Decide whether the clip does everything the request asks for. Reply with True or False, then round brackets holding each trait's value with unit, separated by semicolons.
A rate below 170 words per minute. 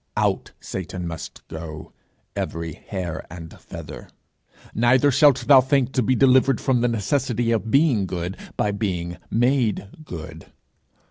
True (135 wpm)